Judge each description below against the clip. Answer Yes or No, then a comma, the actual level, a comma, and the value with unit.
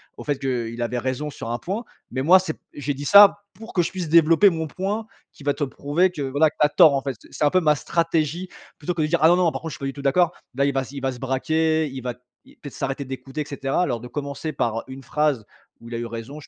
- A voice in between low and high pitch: Yes, medium, 145 Hz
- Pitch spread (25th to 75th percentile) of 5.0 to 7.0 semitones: No, average, 3.8 semitones